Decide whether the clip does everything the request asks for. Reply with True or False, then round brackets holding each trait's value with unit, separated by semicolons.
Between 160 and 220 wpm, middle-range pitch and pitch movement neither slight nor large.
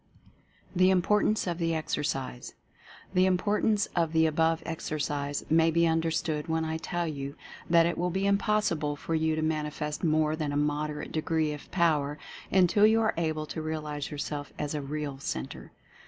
False (170 wpm; 160 Hz; 2.3 semitones)